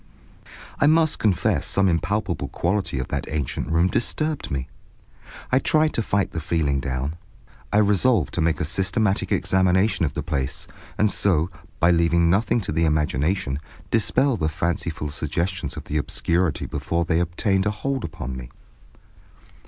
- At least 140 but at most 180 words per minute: Yes, average, 155 wpm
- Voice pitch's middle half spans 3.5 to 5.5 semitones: Yes, average, 4.9 semitones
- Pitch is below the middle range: Yes, very low, 85 Hz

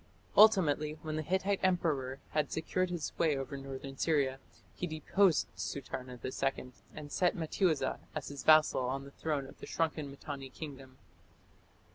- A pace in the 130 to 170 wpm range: Yes, average, 150 wpm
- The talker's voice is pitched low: No, medium, 150 Hz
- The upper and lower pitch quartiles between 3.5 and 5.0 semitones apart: No, average, 3.1 semitones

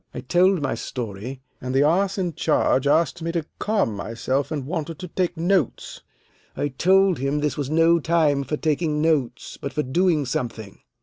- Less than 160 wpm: No, average, 180 wpm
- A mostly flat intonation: No, average, 4.2 semitones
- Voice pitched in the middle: Yes, medium, 150 Hz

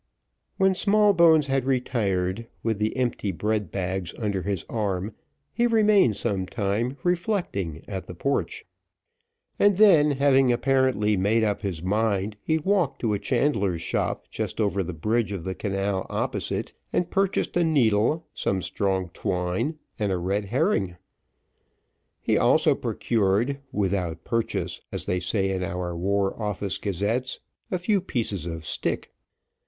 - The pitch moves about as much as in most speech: No, wide, 6.3 semitones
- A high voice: No, low, 105 Hz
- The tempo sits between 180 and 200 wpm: No, average, 145 wpm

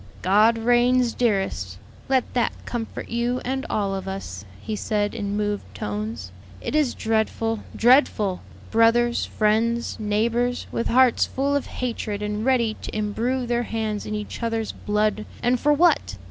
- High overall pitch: Yes, high, 225 Hz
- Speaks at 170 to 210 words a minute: No, average, 150 wpm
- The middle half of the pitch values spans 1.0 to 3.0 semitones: Yes, average, 2.7 semitones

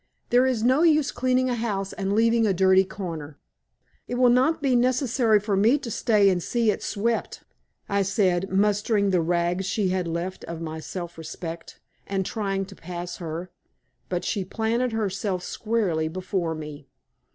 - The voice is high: Yes, high, 195 Hz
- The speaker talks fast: No, average, 170 wpm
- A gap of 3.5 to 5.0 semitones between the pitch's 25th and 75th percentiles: Yes, average, 4.6 semitones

